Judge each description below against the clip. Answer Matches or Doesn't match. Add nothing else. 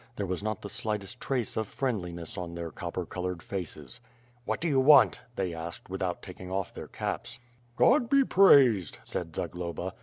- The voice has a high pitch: Doesn't match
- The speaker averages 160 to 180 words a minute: Matches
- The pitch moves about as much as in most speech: Doesn't match